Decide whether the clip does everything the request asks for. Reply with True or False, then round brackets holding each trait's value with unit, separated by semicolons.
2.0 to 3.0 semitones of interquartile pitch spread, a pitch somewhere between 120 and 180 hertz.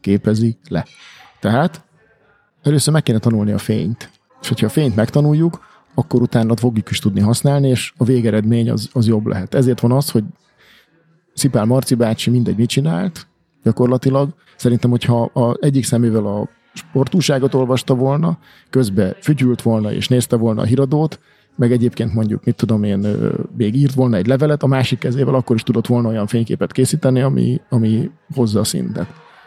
False (3.4 semitones; 125 Hz)